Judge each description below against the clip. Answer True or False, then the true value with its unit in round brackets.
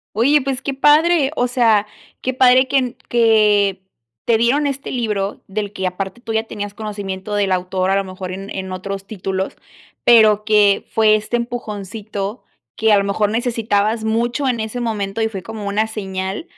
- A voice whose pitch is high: True (215 Hz)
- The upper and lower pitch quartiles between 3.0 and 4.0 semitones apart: True (3.3 semitones)